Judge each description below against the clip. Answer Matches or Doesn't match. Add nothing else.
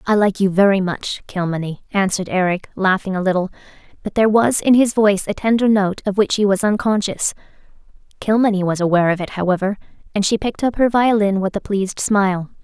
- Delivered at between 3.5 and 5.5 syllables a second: Doesn't match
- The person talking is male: Doesn't match